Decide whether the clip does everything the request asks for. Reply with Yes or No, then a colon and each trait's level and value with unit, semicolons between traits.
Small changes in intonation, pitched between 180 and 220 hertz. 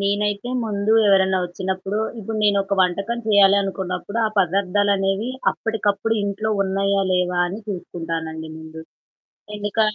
Yes: narrow, 1.8 semitones; high, 195 Hz